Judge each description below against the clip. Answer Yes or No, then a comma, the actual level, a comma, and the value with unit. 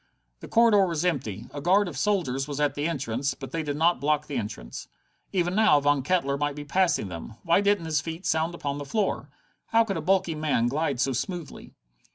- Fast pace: Yes, fast, 210 wpm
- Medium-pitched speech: Yes, medium, 150 Hz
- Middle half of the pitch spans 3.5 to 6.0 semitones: Yes, average, 4.4 semitones